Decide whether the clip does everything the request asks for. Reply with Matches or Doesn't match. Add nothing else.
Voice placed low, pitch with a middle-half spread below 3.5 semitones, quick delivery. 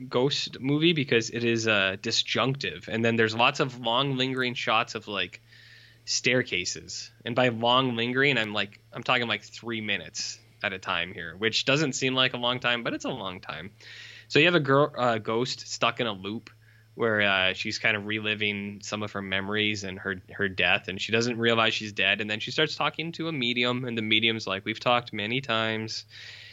Matches